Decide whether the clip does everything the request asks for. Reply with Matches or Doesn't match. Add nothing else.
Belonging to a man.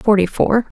Doesn't match